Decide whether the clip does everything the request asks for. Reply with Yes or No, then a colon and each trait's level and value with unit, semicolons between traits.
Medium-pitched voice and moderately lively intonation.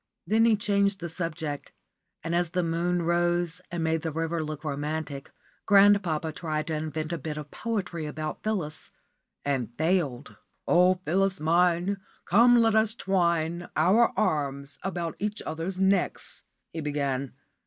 Yes: medium, 170 Hz; average, 3.6 semitones